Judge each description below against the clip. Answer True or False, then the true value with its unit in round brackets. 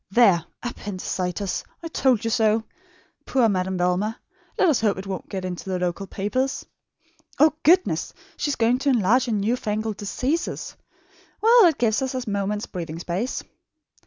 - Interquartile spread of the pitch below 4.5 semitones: False (5.1 semitones)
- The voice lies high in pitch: True (215 Hz)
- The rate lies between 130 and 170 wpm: True (160 wpm)